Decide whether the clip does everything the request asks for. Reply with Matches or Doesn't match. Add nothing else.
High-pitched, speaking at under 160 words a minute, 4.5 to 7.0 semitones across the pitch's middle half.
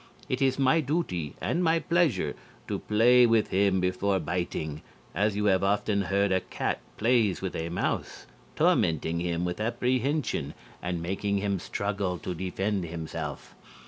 Doesn't match